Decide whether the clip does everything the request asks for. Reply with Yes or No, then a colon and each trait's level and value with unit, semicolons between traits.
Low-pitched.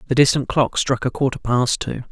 Yes: low, 130 Hz